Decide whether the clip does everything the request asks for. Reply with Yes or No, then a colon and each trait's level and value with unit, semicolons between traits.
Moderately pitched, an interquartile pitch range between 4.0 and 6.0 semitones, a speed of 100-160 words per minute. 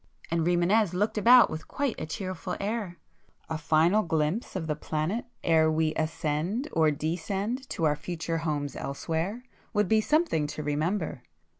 Yes: medium, 165 Hz; average, 4.9 semitones; average, 150 wpm